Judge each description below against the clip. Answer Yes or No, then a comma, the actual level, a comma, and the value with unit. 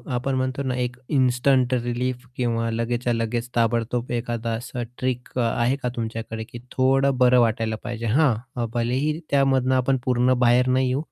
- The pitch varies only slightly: Yes, narrow, 1.6 semitones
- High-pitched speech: No, low, 125 Hz